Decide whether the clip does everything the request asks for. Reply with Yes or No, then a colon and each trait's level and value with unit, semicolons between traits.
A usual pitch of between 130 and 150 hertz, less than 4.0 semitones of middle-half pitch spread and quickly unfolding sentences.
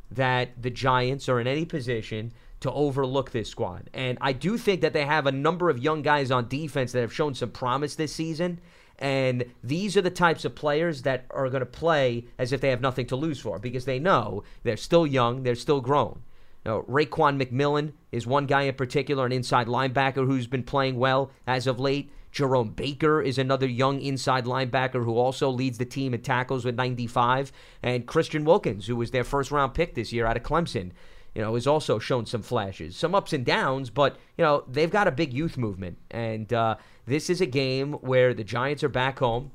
Yes: low, 135 Hz; average, 3.1 semitones; fast, 215 wpm